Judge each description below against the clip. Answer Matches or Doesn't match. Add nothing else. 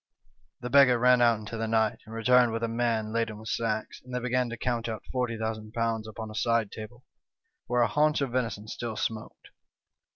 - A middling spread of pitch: Doesn't match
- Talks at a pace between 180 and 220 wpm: Matches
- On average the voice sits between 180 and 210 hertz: Doesn't match